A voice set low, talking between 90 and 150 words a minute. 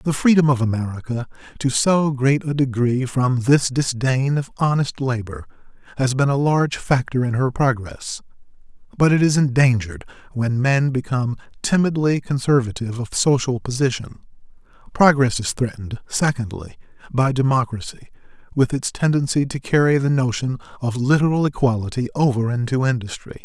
Yes: low, 130 Hz; average, 140 wpm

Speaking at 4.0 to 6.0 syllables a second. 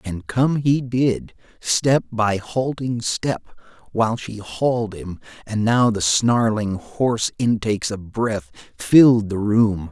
No: 3.7 syllables/s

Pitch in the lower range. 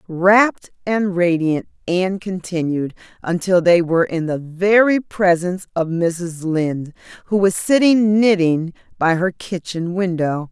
No: medium, 180 Hz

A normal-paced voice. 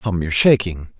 Yes: average, 180 wpm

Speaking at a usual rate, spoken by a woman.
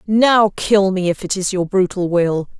No: fast, 210 wpm; female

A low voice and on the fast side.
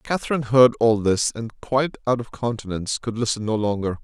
No: low, 115 Hz; average, 195 wpm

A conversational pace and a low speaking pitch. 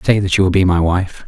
No: fast, 330 wpm; very low, 95 Hz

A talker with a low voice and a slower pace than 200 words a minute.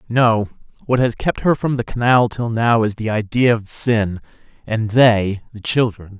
Yes: low, 115 Hz; average, 185 wpm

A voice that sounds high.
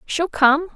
Yes: very high, 315 Hz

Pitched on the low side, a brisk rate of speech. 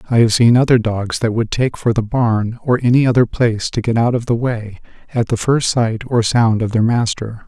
Yes: low, 115 Hz; fast, 240 wpm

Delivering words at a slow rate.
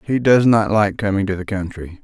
No: fast, 235 wpm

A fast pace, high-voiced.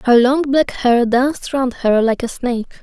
Yes: fast, 210 wpm; very high, 250 Hz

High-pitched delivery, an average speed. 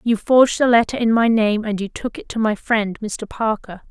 No: high, 225 Hz; fast, 245 wpm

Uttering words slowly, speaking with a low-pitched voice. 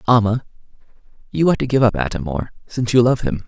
No: fast, 205 wpm; low, 110 Hz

